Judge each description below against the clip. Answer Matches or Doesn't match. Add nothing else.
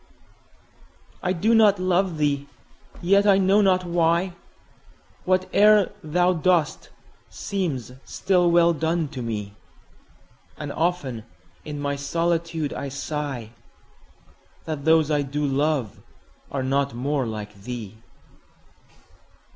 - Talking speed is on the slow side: Matches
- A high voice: Doesn't match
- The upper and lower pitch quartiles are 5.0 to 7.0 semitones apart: Doesn't match